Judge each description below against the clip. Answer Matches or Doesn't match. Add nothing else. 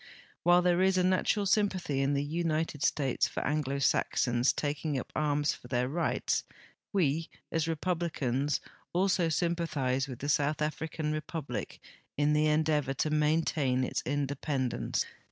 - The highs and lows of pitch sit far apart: Doesn't match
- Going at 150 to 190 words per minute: Doesn't match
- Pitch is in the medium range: Matches